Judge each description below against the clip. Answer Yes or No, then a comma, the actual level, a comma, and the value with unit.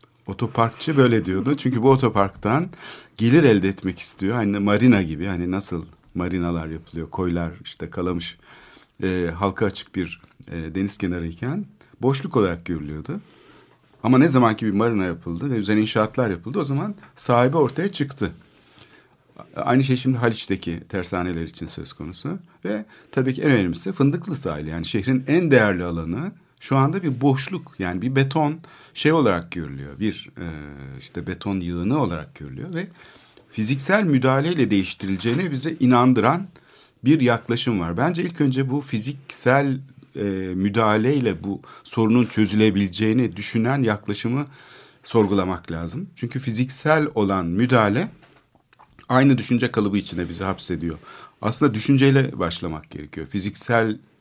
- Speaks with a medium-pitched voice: No, low, 110 Hz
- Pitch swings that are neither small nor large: No, wide, 6.4 semitones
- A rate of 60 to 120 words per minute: No, average, 130 wpm